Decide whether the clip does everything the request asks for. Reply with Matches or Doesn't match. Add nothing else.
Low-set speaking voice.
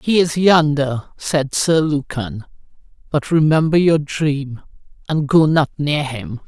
Doesn't match